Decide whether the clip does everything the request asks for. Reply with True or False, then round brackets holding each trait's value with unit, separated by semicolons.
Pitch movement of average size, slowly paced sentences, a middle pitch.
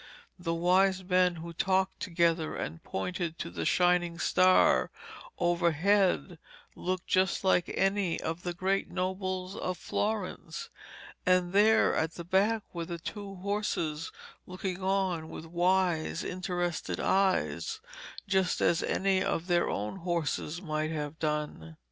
False (2.2 semitones; 130 wpm; 180 Hz)